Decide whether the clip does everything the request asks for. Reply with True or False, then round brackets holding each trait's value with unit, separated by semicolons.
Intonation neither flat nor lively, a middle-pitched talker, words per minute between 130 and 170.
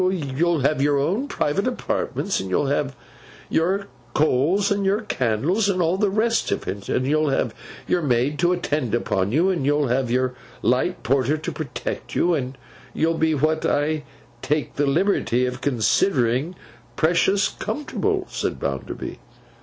False (5.7 semitones; 150 Hz; 160 wpm)